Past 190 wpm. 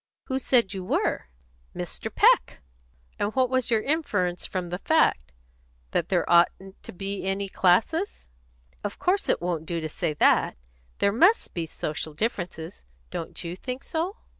No: average, 160 wpm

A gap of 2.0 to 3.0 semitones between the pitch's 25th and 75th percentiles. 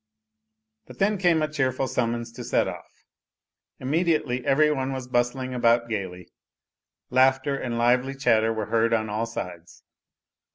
Yes: average, 2.7 semitones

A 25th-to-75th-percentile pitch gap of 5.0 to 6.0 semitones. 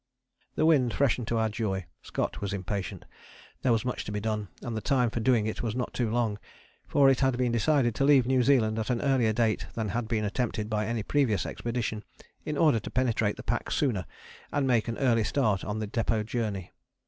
No: average, 2.9 semitones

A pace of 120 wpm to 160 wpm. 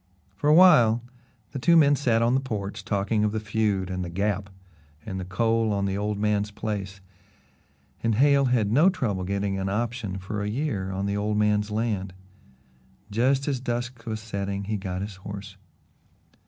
No: average, 180 wpm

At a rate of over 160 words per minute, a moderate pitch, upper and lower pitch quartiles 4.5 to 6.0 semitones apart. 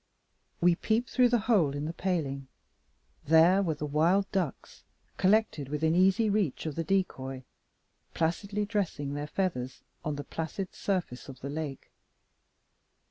No: average, 140 wpm; medium, 165 Hz; average, 5.2 semitones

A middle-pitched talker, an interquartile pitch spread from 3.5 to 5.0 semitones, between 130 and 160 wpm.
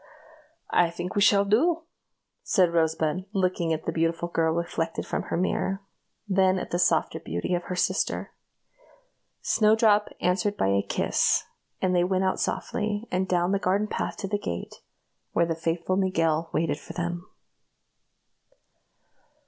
No: medium, 180 Hz; average, 2.8 semitones; average, 150 wpm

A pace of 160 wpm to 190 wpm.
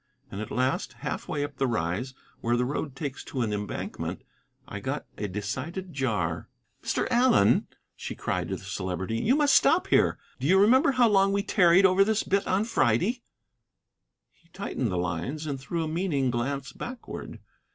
Yes: average, 180 wpm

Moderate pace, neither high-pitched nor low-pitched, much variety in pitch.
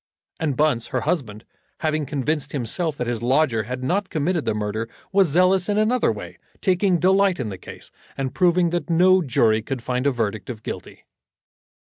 Yes: average, 180 wpm; medium, 145 Hz; wide, 7.1 semitones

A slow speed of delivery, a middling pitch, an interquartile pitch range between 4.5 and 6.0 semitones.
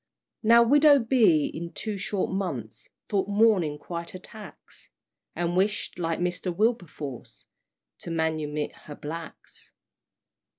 Yes: slow, 120 wpm; medium, 180 Hz; average, 4.9 semitones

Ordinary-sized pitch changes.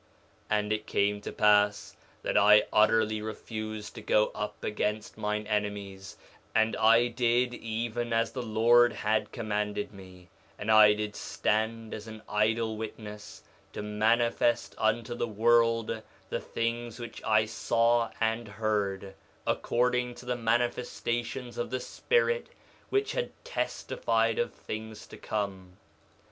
No: narrow, 2.0 semitones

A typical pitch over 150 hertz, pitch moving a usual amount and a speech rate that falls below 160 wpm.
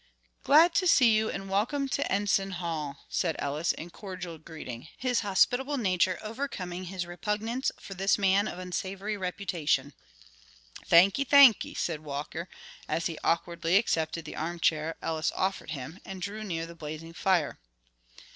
Yes: medium, 185 Hz; average, 4.1 semitones; average, 150 wpm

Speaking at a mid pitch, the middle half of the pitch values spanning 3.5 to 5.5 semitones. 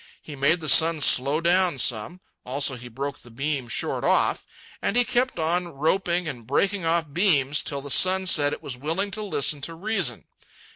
Yes: medium, 155 Hz; average, 4.6 semitones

